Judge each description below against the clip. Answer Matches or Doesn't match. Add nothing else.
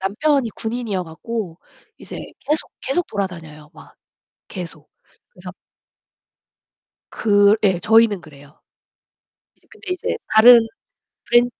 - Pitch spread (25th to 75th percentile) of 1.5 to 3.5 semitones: Doesn't match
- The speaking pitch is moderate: Doesn't match